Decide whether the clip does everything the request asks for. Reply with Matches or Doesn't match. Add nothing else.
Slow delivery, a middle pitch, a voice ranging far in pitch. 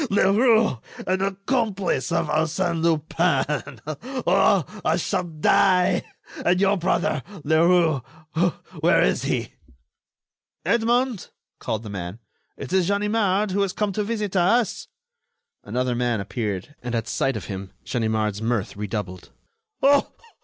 Matches